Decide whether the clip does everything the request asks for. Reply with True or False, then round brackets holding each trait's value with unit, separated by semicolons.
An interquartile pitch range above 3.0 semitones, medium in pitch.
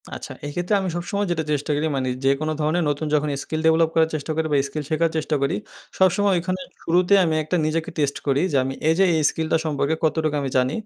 False (2.6 semitones; 160 Hz)